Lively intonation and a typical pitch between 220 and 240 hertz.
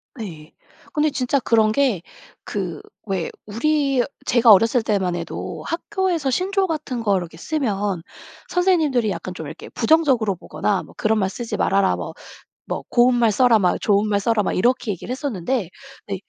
Yes: wide, 5.8 semitones; high, 225 Hz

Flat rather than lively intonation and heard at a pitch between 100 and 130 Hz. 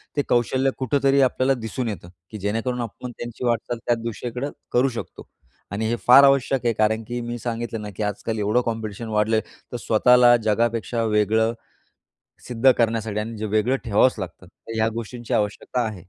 Yes: narrow, 2.3 semitones; low, 115 Hz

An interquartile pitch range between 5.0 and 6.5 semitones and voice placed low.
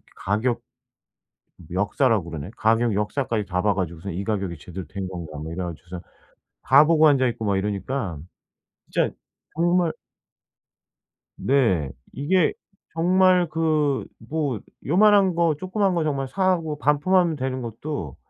No: wide, 8.7 semitones; low, 130 Hz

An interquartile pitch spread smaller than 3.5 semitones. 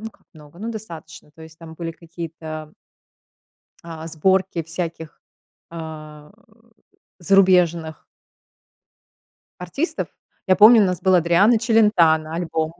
Yes: average, 2.9 semitones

